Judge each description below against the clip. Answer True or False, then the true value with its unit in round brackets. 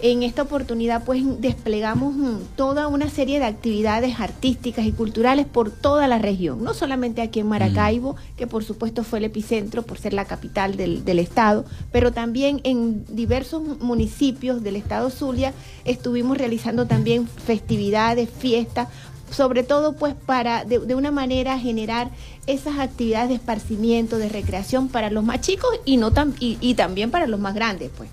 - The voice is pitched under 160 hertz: False (235 Hz)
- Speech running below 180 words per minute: True (165 wpm)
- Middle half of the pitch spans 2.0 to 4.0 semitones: True (3.1 semitones)